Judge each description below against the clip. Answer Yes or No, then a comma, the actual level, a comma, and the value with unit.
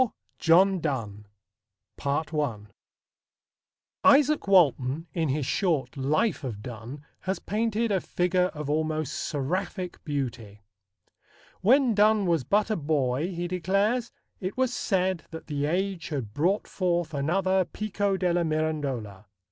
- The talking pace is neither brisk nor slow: No, slow, 125 wpm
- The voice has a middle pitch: Yes, medium, 170 Hz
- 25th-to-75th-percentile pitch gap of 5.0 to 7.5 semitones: Yes, wide, 5.4 semitones